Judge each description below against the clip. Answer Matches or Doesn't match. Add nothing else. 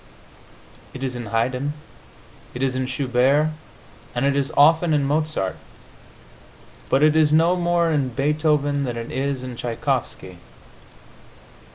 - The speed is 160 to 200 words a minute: Doesn't match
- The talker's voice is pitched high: Doesn't match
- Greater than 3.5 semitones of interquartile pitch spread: Doesn't match